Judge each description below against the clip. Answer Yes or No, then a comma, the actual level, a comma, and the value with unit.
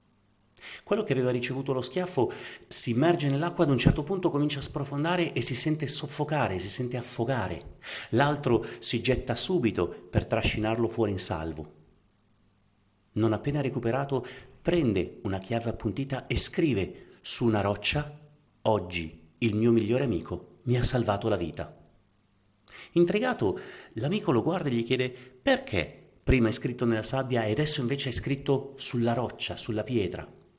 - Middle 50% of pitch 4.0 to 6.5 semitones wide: Yes, average, 4.7 semitones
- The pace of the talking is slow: No, average, 150 wpm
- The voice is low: Yes, low, 120 Hz